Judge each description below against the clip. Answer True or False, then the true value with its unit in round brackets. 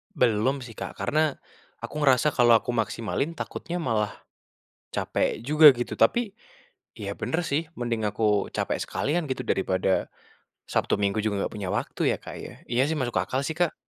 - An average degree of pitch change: False (5.9 semitones)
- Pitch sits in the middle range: False (125 Hz)